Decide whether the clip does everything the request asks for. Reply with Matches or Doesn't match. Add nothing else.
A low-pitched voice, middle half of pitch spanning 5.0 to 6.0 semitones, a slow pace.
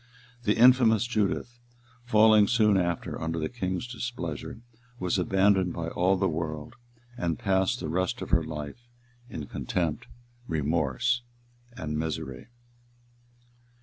Matches